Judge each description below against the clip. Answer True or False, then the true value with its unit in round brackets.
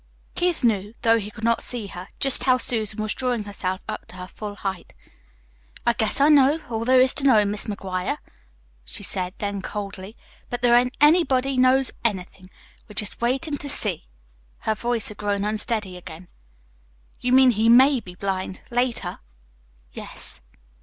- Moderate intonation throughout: True (4.1 semitones)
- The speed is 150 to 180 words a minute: True (170 wpm)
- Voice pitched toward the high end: True (220 Hz)